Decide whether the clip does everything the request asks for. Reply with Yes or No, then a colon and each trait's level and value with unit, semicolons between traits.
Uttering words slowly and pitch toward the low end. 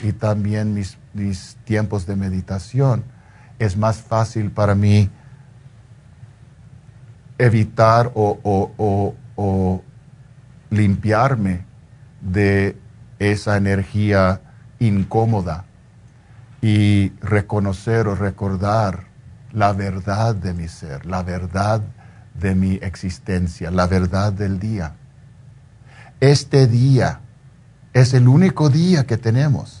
Yes: slow, 95 wpm; low, 110 Hz